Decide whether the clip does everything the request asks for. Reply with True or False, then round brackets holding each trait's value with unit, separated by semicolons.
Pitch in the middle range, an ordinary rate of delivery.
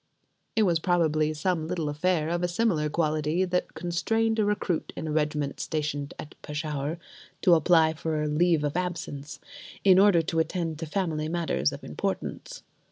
True (160 Hz; 165 wpm)